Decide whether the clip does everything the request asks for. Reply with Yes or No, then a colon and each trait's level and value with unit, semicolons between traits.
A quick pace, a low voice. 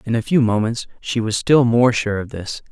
Yes: fast, 245 wpm; low, 115 Hz